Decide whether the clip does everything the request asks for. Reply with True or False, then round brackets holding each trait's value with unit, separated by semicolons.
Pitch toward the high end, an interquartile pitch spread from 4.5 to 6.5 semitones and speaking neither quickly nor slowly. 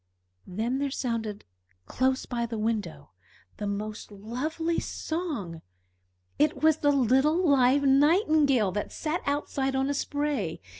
False (265 Hz; 5.1 semitones; 130 wpm)